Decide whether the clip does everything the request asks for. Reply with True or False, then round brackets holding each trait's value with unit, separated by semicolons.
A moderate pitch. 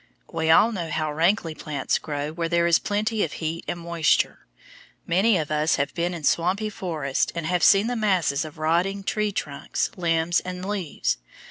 True (170 Hz)